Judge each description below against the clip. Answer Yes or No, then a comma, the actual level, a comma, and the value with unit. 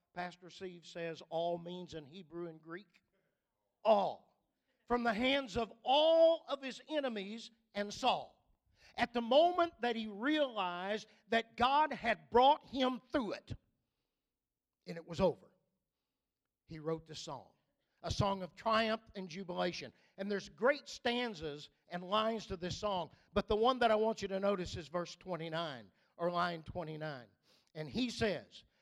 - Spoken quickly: No, average, 155 wpm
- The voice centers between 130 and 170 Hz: No, high, 200 Hz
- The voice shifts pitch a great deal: Yes, wide, 5.8 semitones